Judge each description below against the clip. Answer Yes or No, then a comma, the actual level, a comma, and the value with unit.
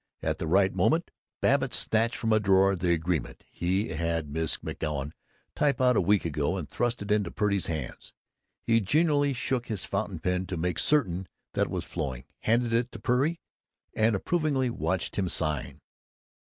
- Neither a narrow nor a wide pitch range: No, wide, 6.2 semitones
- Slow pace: No, average, 175 wpm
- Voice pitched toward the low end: Yes, low, 100 Hz